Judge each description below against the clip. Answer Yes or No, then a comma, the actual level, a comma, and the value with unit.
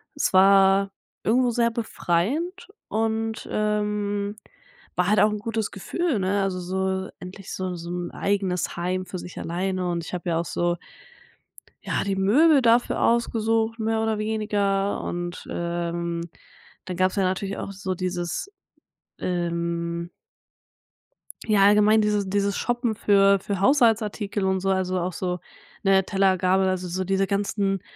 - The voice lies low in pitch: No, high, 195 Hz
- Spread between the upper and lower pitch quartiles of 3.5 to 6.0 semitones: No, average, 2.7 semitones